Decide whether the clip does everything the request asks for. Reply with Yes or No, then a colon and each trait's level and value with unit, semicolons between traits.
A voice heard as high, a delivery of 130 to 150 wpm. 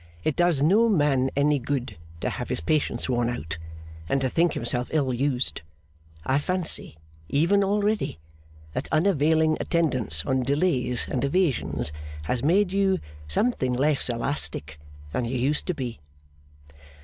No: medium, 140 Hz; average, 140 wpm